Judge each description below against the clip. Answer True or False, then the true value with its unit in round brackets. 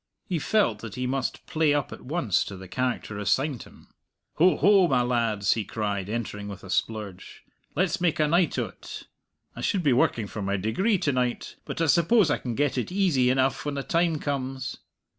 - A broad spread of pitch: True (6.9 semitones)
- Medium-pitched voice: False (130 Hz)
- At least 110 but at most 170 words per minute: False (200 wpm)